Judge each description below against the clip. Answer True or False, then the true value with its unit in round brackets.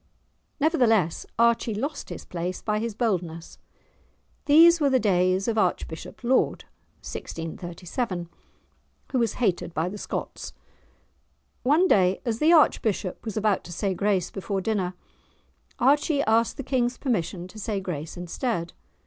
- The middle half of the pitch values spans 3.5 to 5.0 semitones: False (5.4 semitones)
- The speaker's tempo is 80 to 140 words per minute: True (135 wpm)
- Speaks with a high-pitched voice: True (210 Hz)